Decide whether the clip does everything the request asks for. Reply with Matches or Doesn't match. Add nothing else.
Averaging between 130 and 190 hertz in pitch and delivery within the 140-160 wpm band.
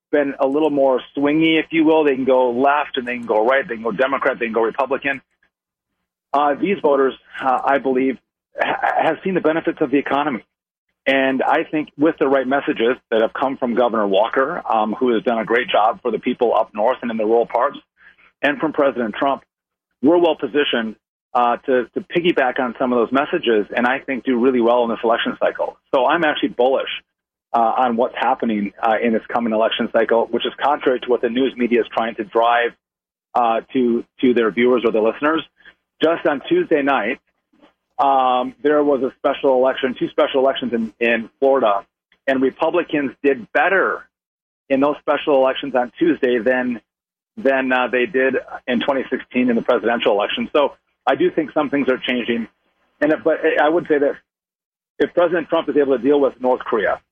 Doesn't match